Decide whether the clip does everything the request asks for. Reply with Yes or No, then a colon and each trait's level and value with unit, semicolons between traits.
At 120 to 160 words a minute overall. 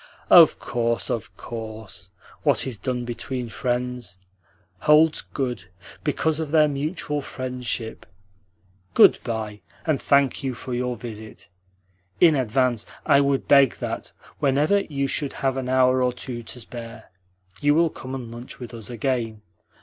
Yes: average, 145 wpm